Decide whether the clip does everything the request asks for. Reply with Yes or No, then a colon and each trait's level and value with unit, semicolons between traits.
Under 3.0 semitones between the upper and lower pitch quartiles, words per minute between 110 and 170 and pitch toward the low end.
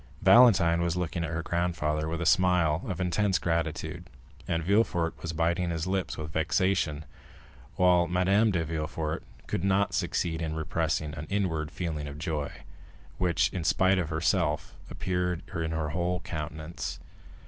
Yes: narrow, 2.4 semitones; average, 150 wpm; very low, 85 Hz